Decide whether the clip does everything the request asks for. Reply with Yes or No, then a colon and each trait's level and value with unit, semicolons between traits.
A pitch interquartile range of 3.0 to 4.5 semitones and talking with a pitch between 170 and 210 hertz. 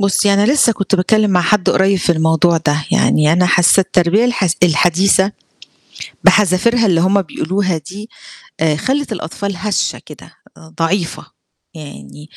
Yes: average, 3.6 semitones; medium, 185 Hz